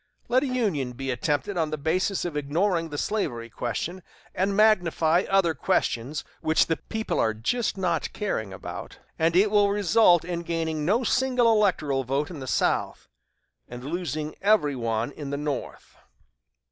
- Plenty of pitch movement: Yes, wide, 6.0 semitones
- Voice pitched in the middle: Yes, medium, 165 Hz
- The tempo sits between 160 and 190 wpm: Yes, average, 165 wpm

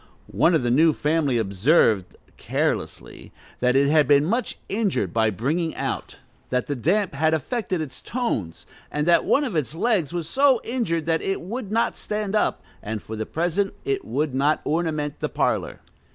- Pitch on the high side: No, medium, 160 Hz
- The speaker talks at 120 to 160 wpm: No, average, 180 wpm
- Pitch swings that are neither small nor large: No, wide, 6.6 semitones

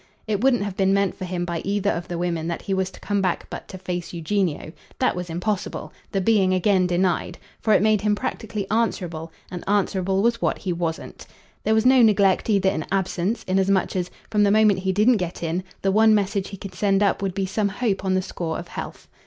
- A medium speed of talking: No, fast, 225 wpm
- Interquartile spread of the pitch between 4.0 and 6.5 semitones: No, narrow, 2.4 semitones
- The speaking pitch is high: Yes, high, 195 Hz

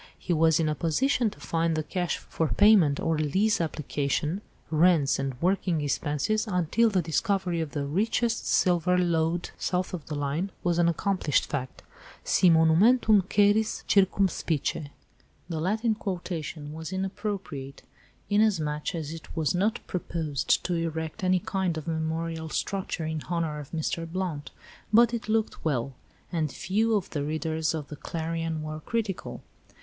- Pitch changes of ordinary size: Yes, average, 3.8 semitones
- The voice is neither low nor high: Yes, medium, 165 Hz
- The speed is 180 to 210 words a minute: No, average, 150 wpm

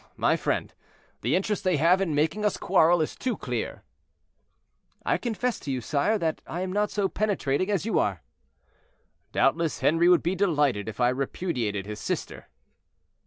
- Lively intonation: Yes, wide, 6.0 semitones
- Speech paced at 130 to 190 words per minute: Yes, average, 170 wpm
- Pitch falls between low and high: Yes, medium, 170 Hz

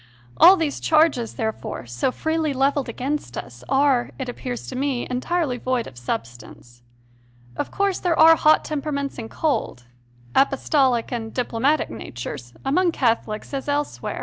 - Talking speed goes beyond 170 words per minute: No, average, 150 wpm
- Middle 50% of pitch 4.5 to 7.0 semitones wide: Yes, average, 4.9 semitones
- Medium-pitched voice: No, very high, 265 Hz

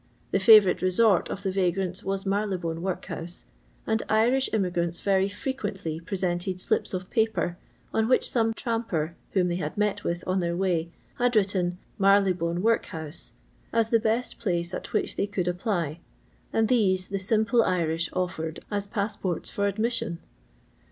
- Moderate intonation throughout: Yes, average, 3.7 semitones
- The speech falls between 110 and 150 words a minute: No, average, 160 wpm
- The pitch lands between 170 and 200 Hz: Yes, high, 190 Hz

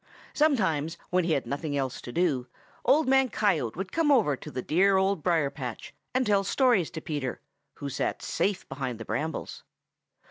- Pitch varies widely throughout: Yes, wide, 6.6 semitones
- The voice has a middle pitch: Yes, medium, 165 Hz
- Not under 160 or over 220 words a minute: Yes, average, 180 wpm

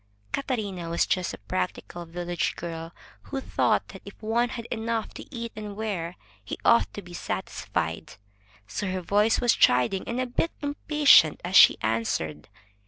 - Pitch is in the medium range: No, high, 195 Hz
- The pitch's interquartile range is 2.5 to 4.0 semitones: No, wide, 5.6 semitones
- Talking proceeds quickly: No, average, 165 wpm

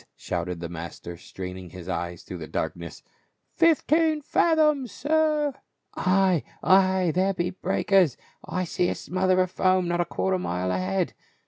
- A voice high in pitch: No, medium, 180 Hz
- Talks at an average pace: Yes, average, 160 wpm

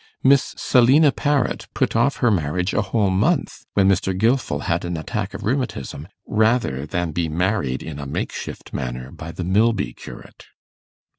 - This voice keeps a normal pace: Yes, average, 160 wpm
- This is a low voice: Yes, very low, 95 Hz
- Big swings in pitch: Yes, wide, 7.1 semitones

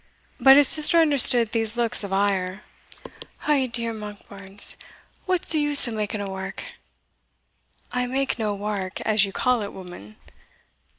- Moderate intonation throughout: Yes, average, 4.5 semitones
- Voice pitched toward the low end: No, high, 220 Hz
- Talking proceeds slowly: No, average, 145 wpm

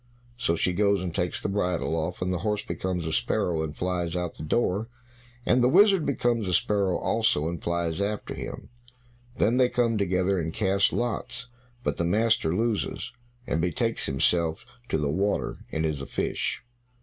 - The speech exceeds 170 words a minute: Yes, average, 185 wpm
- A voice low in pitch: Yes, very low, 90 Hz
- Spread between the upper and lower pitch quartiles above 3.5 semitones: Yes, average, 4.7 semitones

